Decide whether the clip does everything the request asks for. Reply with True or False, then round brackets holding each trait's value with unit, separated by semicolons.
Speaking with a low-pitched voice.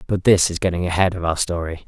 True (90 Hz)